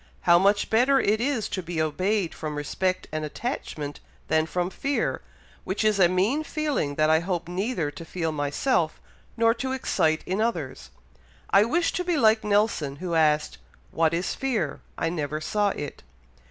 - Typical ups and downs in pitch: No, wide, 5.9 semitones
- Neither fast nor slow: Yes, average, 170 wpm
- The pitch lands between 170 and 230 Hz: Yes, medium, 185 Hz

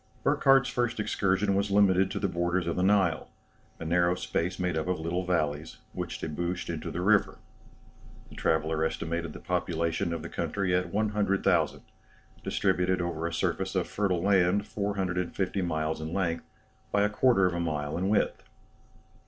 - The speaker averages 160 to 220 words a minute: Yes, average, 165 wpm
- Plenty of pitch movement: No, average, 2.9 semitones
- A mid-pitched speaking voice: No, very low, 90 Hz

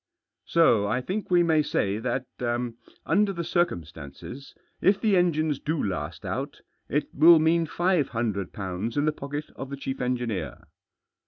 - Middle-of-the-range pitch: Yes, medium, 145 Hz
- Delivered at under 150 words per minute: No, average, 160 wpm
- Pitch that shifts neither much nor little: No, wide, 6.5 semitones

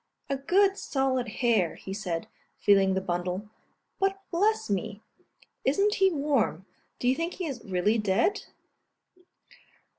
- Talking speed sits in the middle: No, slow, 130 wpm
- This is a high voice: Yes, high, 240 Hz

